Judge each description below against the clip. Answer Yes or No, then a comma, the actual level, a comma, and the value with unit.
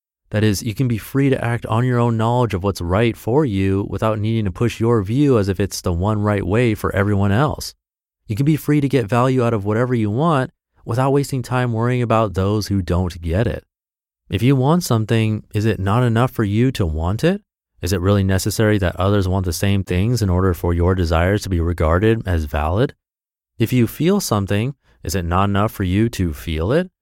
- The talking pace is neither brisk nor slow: No, fast, 225 wpm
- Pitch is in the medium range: No, low, 105 Hz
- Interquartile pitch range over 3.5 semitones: Yes, average, 4.1 semitones